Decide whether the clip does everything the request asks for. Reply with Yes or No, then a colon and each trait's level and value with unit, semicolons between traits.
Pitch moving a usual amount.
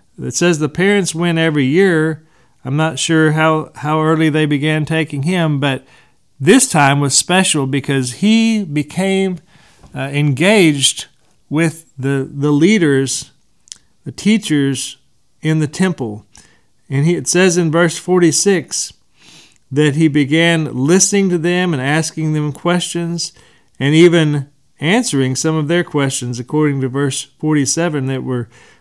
Yes: average, 3.7 semitones